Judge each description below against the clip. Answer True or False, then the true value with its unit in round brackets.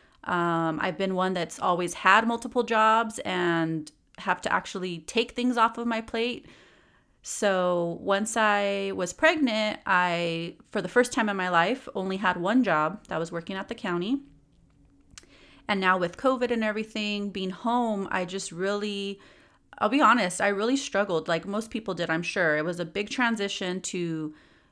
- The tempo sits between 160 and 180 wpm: True (170 wpm)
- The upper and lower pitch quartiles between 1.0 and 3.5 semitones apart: False (4.1 semitones)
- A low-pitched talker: False (195 Hz)